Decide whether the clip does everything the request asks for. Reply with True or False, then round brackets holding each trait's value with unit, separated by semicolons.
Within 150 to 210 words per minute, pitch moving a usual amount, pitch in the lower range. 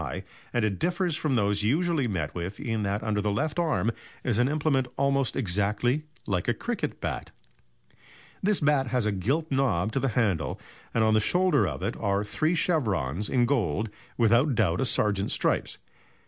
False (180 wpm; 5.8 semitones; 115 Hz)